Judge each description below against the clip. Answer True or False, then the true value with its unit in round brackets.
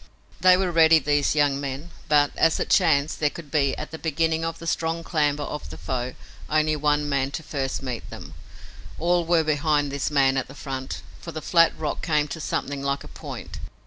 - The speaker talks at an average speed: False (210 wpm)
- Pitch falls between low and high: True (150 Hz)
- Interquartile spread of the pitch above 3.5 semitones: False (2.5 semitones)